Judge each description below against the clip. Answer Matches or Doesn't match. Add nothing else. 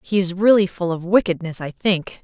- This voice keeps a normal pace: Doesn't match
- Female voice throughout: Matches